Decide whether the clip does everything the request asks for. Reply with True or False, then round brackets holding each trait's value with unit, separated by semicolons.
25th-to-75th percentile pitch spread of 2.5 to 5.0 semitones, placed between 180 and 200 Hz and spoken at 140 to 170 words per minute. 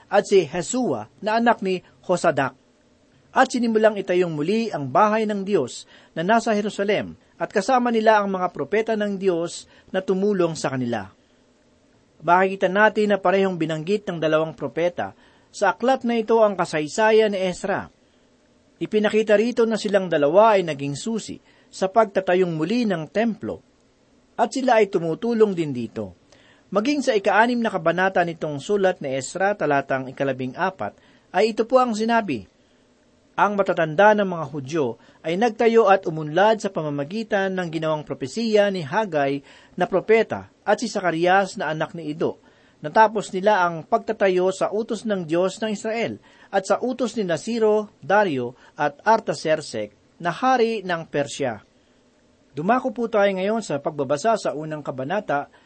False (5.4 semitones; 190 Hz; 150 wpm)